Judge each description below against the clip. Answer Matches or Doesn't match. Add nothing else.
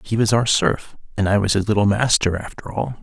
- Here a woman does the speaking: Doesn't match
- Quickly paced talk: Matches